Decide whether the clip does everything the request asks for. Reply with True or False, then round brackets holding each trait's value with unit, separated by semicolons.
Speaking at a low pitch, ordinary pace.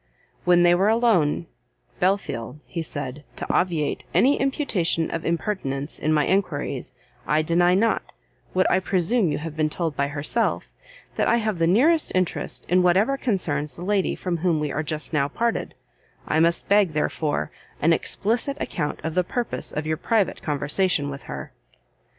False (170 Hz; 170 wpm)